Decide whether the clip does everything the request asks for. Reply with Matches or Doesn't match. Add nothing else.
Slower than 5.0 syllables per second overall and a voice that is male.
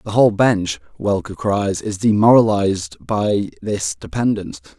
Matches